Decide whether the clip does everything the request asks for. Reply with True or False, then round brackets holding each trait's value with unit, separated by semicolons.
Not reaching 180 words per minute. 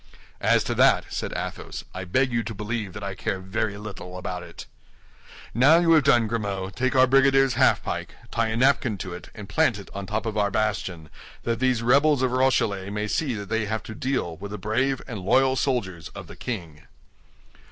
False (205 wpm)